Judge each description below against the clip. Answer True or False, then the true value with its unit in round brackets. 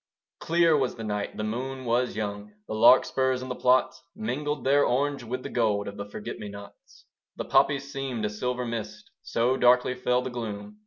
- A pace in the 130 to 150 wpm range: False (195 wpm)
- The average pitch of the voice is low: True (125 Hz)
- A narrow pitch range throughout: False (3.5 semitones)